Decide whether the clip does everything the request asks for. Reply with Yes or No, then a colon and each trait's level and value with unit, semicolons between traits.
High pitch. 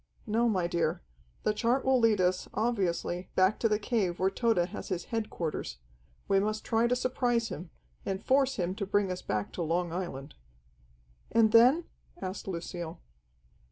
Yes: high, 200 Hz